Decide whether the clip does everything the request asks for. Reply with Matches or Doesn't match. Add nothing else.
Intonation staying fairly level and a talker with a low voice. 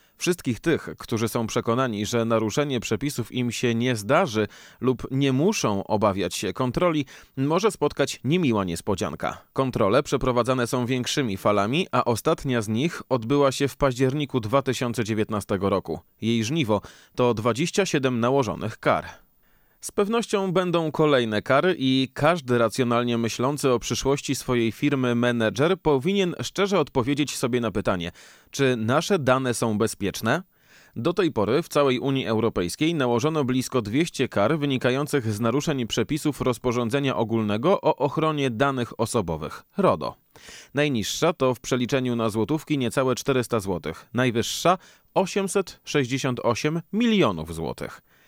Doesn't match